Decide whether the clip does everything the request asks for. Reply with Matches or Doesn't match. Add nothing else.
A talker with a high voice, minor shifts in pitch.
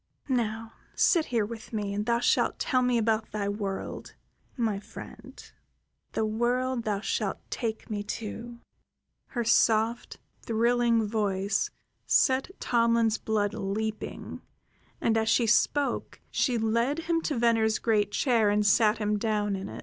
Matches